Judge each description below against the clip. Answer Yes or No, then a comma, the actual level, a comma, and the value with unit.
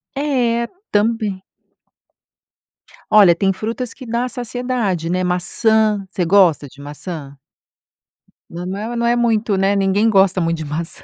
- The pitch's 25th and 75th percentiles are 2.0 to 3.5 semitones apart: No, average, 4.6 semitones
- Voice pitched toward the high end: Yes, high, 200 Hz